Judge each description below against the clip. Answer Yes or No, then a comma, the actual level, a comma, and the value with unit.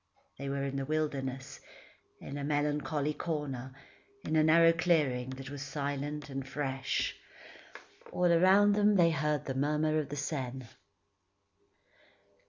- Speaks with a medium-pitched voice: Yes, medium, 145 Hz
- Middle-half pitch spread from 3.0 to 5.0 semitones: No, narrow, 2.4 semitones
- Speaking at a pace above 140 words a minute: No, slow, 135 wpm